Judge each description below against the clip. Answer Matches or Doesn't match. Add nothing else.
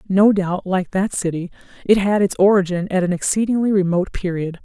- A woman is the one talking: Matches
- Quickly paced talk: Doesn't match